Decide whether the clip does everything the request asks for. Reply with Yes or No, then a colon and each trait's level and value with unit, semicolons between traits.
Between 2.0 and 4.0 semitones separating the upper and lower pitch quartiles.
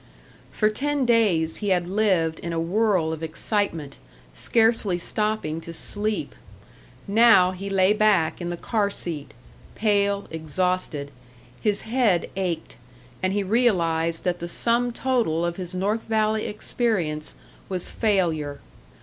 No: average, 4.4 semitones